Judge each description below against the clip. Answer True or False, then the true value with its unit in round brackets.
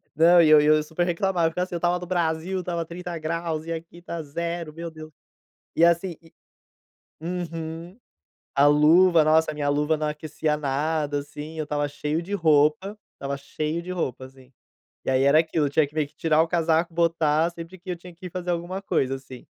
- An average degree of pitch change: False (2.3 semitones)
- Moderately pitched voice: True (160 Hz)